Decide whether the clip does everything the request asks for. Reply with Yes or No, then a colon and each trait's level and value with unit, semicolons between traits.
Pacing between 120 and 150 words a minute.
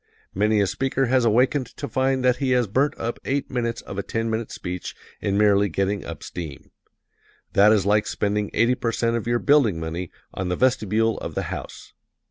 No: average, 195 wpm